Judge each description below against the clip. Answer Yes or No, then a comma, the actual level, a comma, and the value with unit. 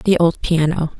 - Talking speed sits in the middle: Yes, average, 180 wpm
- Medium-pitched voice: Yes, medium, 165 Hz